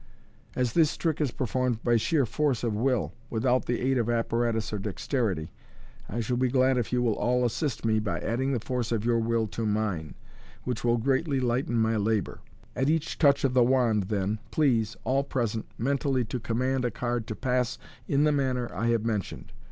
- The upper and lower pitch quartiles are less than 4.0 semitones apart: Yes, average, 2.7 semitones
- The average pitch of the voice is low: Yes, low, 120 Hz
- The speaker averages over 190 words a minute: Yes, average, 200 wpm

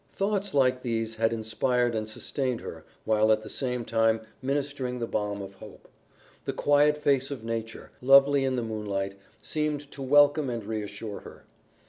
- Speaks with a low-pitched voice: Yes, low, 120 Hz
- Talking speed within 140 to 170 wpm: Yes, average, 165 wpm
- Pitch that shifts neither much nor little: Yes, average, 4.0 semitones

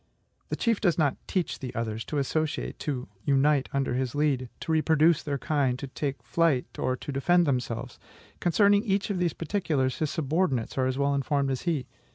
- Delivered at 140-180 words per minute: No, average, 195 wpm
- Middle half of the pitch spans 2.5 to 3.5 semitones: No, average, 4.1 semitones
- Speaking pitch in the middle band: Yes, medium, 145 Hz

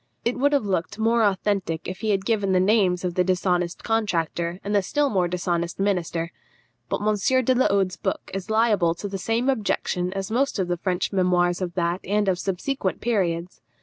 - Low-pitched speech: No, high, 190 Hz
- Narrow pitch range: No, average, 3.4 semitones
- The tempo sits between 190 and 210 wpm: Yes, average, 200 wpm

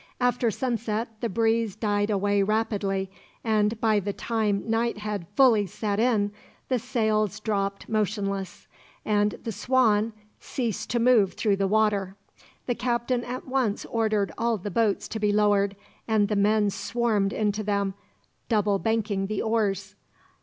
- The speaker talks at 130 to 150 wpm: Yes, average, 145 wpm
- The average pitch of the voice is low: No, high, 215 Hz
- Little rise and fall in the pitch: Yes, narrow, 2.1 semitones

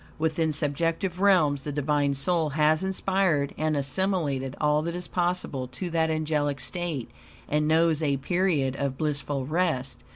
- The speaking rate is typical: Yes, average, 150 wpm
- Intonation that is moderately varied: Yes, average, 3.3 semitones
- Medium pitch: Yes, medium, 155 Hz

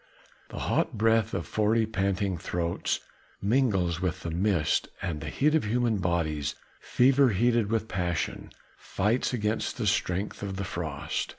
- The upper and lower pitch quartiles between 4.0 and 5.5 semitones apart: Yes, average, 4.4 semitones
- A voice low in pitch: Yes, low, 100 Hz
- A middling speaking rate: Yes, average, 150 wpm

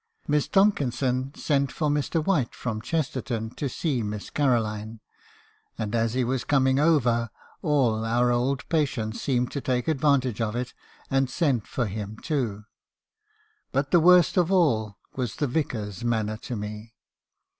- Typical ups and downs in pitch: Yes, average, 4.3 semitones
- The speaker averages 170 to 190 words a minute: No, average, 150 wpm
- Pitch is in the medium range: No, low, 125 Hz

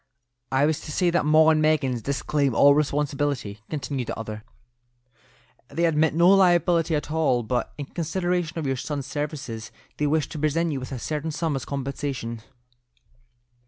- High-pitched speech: No, medium, 150 Hz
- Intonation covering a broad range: No, average, 3.0 semitones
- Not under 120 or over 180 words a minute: Yes, average, 165 wpm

